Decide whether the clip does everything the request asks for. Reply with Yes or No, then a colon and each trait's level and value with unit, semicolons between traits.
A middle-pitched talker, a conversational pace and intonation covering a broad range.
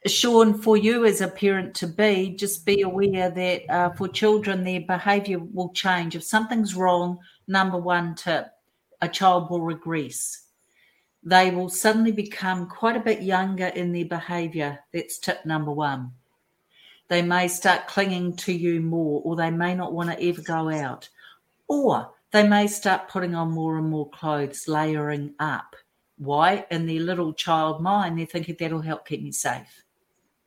No: medium, 180 Hz; average, 165 wpm; average, 2.7 semitones